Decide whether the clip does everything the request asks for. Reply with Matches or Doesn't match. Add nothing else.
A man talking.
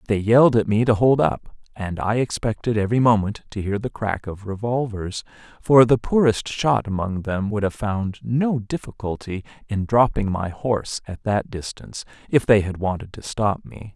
Matches